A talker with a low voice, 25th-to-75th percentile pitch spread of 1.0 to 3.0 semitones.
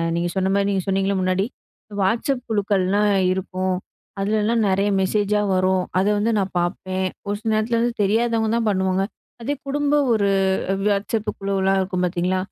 No: high, 195 Hz; narrow, 2.4 semitones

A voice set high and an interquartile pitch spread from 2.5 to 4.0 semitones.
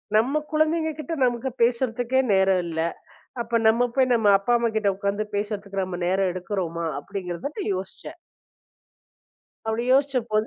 No: high, 220 Hz; average, 4.6 semitones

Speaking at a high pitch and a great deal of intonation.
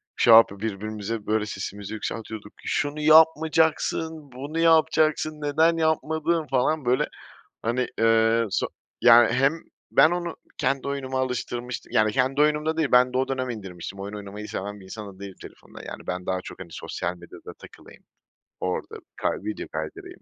No: low, 125 Hz; wide, 6.5 semitones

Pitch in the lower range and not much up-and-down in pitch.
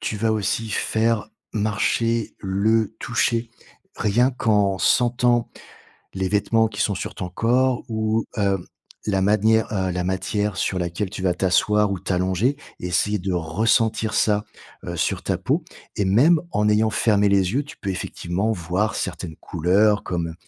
No: low, 105 Hz; average, 3.0 semitones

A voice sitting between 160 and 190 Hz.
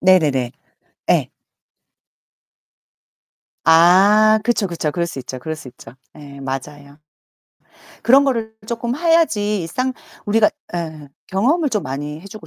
Yes: medium, 185 Hz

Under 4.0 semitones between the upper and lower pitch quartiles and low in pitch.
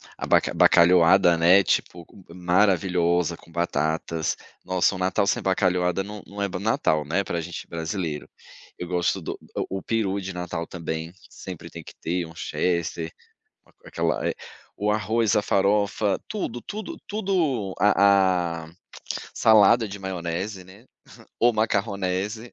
Yes: average, 3.1 semitones; very low, 95 Hz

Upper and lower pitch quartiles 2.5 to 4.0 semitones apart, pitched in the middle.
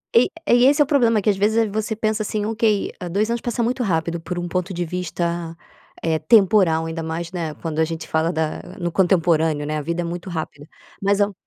No: average, 4.7 semitones; medium, 175 Hz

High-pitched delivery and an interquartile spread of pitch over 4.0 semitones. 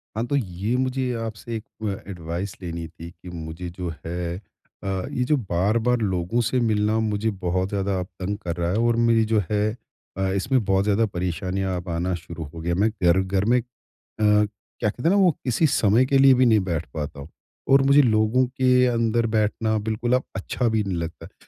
No: low, 105 Hz; average, 4.7 semitones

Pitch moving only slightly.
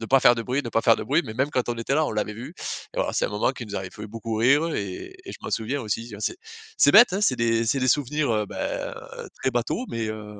No: average, 4.1 semitones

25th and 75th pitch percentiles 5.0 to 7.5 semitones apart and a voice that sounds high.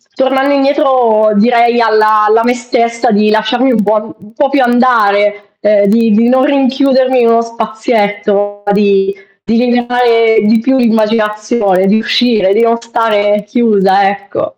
No: average, 2.8 semitones; high, 225 Hz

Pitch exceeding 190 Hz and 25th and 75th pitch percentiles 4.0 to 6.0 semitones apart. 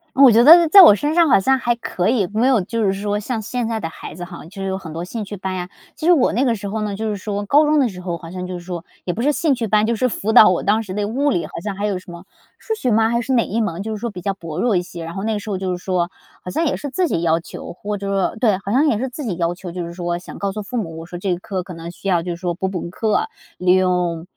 Yes: high, 200 Hz; average, 4.5 semitones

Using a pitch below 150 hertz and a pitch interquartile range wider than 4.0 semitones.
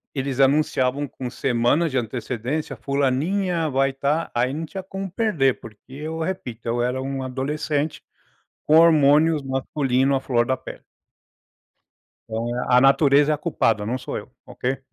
No: low, 135 Hz; average, 3.3 semitones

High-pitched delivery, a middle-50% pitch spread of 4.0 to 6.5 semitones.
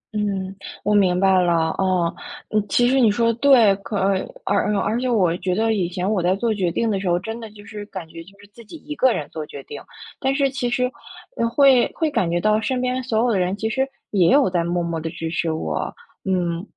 Yes: high, 205 Hz; average, 4.6 semitones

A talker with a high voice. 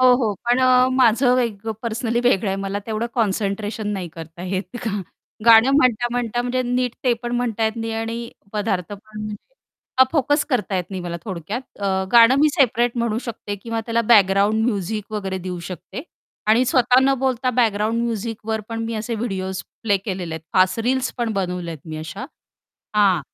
Yes: high, 225 Hz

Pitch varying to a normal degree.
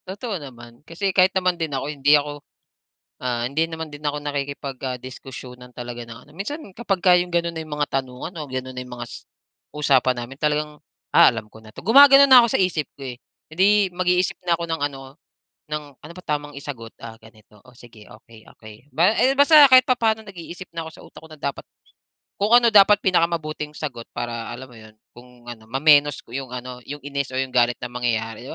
No: wide, 5.7 semitones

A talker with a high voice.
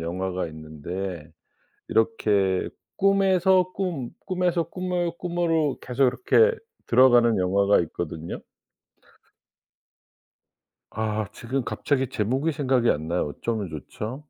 No: low, 120 Hz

